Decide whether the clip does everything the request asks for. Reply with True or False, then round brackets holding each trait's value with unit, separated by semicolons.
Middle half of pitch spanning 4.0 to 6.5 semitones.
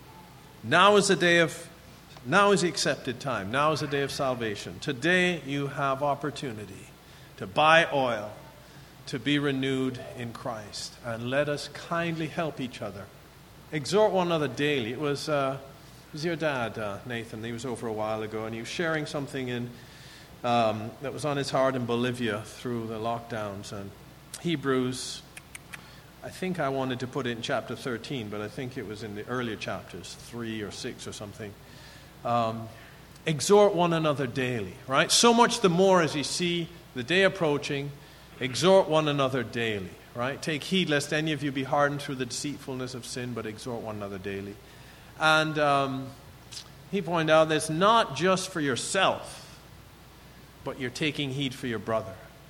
True (4.5 semitones)